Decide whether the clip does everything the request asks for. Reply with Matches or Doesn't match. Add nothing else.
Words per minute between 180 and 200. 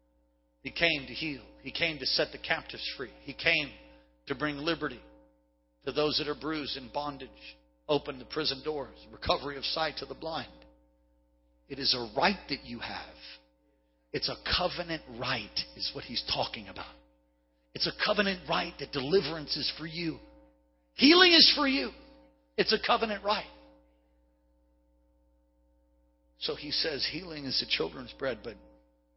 Doesn't match